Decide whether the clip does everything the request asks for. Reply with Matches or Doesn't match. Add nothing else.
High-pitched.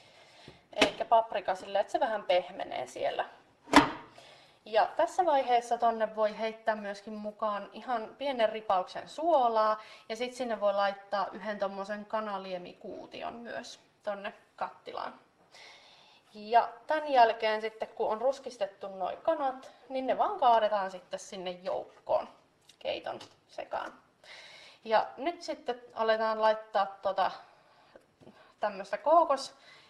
Matches